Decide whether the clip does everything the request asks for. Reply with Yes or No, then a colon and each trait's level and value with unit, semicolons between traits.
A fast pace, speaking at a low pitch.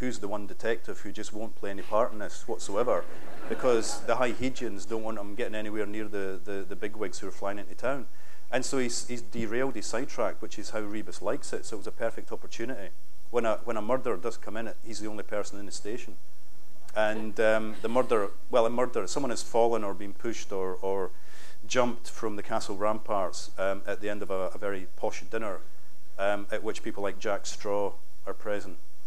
Yes: fast, 220 wpm; low, 110 Hz